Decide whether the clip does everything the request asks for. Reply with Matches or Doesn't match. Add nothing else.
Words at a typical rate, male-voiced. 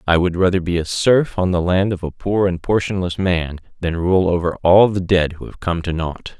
Doesn't match